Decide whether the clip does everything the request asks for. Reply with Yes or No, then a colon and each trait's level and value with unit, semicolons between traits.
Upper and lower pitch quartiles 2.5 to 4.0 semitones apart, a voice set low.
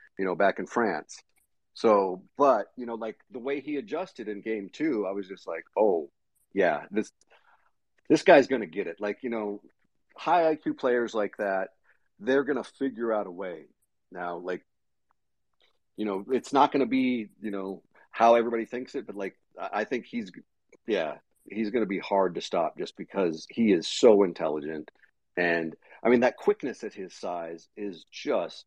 No: average, 4.6 semitones; low, 110 Hz